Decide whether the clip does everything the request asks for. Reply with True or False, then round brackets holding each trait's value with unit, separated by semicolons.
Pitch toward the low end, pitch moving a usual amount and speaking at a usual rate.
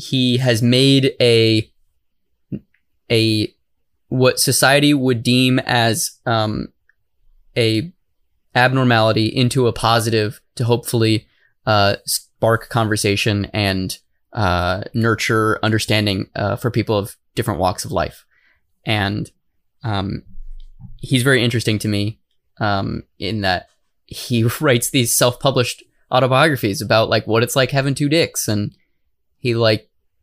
False (115 Hz; 3.0 semitones; 115 wpm)